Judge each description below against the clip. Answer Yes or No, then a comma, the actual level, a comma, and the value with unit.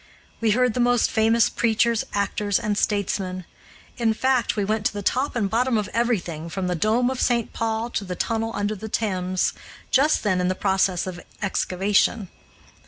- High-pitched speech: Yes, high, 215 Hz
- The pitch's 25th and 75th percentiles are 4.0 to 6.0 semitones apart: No, average, 3.5 semitones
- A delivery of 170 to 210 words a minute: Yes, average, 180 wpm